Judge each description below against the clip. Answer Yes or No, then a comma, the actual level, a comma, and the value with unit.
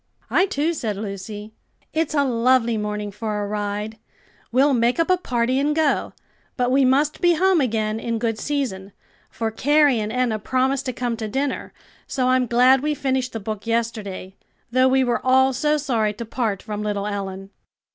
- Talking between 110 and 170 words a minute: No, average, 185 wpm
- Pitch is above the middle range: Yes, high, 240 Hz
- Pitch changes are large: No, average, 4.0 semitones